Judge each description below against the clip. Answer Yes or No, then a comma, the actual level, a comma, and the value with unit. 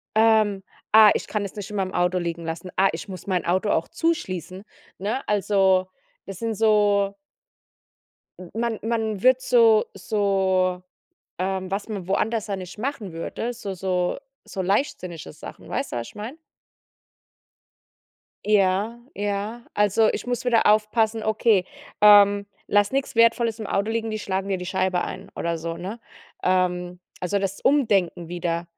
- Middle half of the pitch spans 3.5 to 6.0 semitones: No, average, 3.0 semitones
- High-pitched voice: Yes, high, 200 Hz